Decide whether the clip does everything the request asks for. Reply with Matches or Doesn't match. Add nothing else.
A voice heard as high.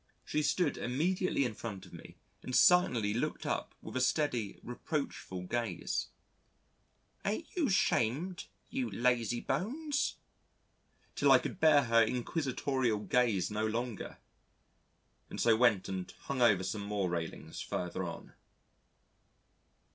Doesn't match